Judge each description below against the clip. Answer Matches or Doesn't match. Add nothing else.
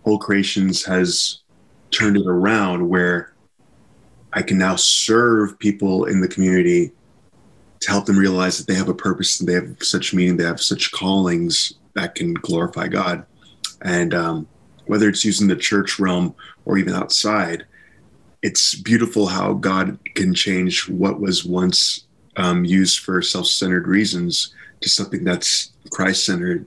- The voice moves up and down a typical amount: Doesn't match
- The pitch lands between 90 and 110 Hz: Matches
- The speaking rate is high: Doesn't match